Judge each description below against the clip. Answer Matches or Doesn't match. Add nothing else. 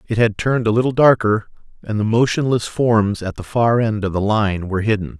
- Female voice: Doesn't match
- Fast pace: Matches